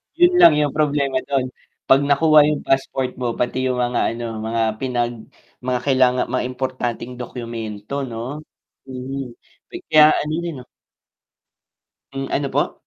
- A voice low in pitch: Yes, low, 130 Hz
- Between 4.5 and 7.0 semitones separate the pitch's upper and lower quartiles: No, narrow, 2.5 semitones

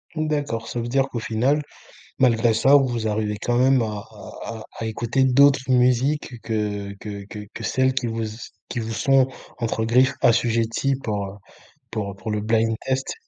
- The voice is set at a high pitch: No, low, 115 Hz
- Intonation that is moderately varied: Yes, average, 3.0 semitones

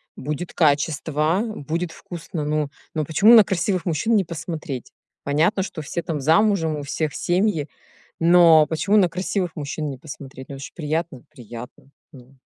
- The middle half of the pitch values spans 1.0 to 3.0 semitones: No, average, 3.4 semitones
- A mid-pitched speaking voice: Yes, medium, 160 Hz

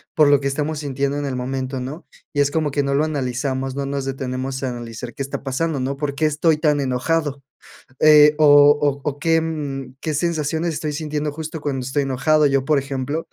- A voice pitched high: No, medium, 140 Hz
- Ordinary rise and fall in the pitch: No, narrow, 2.3 semitones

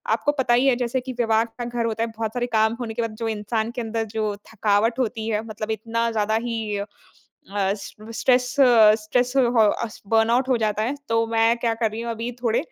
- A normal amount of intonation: No, narrow, 1.6 semitones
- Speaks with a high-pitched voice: Yes, high, 230 Hz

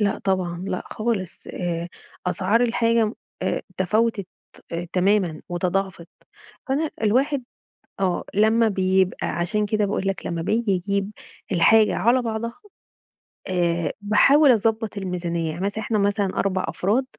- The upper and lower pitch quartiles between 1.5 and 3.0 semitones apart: No, average, 3.5 semitones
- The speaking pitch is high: Yes, high, 200 Hz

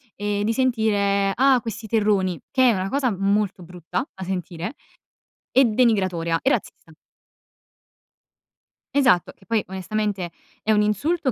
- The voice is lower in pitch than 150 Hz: No, high, 210 Hz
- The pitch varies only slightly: No, average, 3.6 semitones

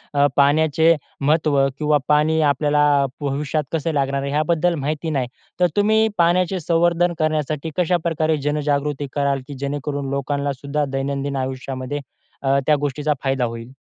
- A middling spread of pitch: No, narrow, 2.3 semitones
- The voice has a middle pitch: Yes, medium, 145 Hz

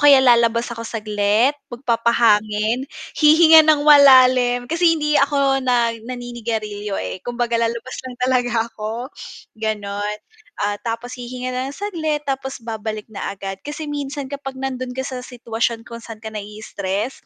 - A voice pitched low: No, high, 245 Hz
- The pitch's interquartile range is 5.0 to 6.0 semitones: No, average, 3.4 semitones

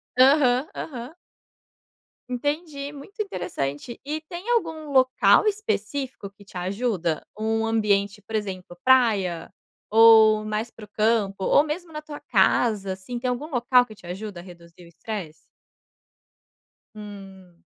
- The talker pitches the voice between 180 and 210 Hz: No, high, 225 Hz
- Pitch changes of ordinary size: No, wide, 6.1 semitones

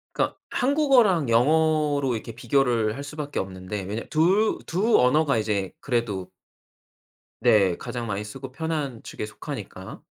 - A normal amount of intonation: No, wide, 6.5 semitones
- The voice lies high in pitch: No, low, 125 Hz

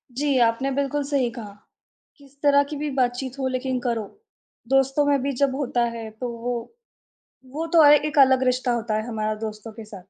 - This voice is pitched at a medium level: No, very high, 260 Hz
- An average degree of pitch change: Yes, average, 3.3 semitones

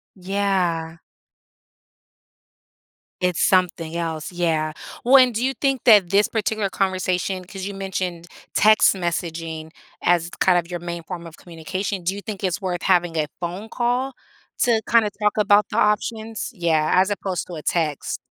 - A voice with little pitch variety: No, average, 3.4 semitones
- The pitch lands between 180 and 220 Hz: Yes, medium, 185 Hz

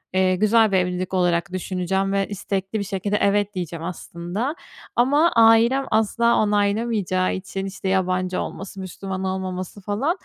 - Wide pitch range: No, narrow, 2.5 semitones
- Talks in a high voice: Yes, high, 195 Hz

